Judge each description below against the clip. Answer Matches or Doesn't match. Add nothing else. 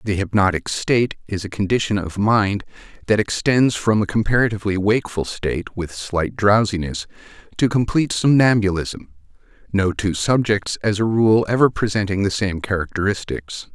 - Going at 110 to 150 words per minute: Matches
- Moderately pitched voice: Doesn't match